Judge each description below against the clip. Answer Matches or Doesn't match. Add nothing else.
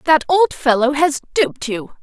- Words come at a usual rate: Matches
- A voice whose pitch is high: Matches